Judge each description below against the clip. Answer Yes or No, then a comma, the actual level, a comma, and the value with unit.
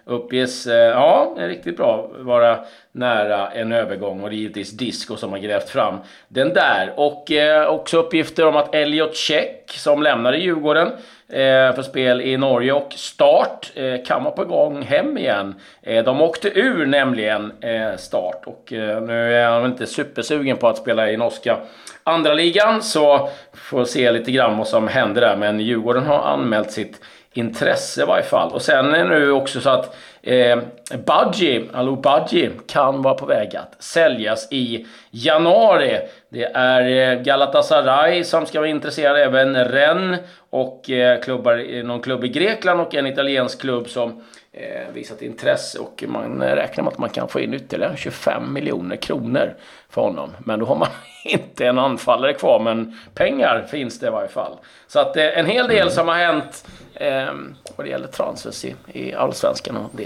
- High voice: No, low, 130 Hz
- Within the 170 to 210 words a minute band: Yes, average, 175 wpm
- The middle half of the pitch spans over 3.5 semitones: Yes, average, 4.0 semitones